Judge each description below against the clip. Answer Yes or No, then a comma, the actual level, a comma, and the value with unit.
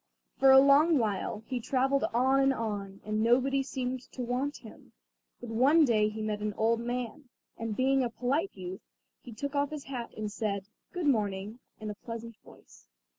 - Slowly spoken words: No, average, 185 wpm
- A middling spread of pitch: Yes, average, 4.1 semitones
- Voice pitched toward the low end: No, high, 240 Hz